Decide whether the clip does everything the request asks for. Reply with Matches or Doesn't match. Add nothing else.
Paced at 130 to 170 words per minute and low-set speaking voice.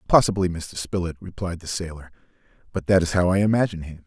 Doesn't match